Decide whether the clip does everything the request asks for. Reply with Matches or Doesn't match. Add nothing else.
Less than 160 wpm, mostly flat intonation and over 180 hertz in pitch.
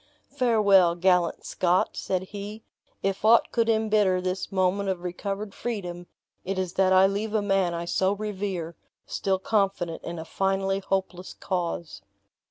Matches